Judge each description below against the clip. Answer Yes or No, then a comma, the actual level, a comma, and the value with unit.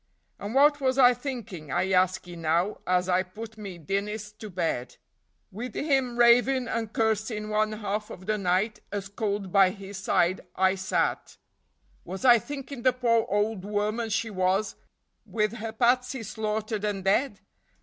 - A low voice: No, high, 210 Hz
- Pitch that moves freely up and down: No, average, 3.5 semitones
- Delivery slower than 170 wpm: Yes, average, 160 wpm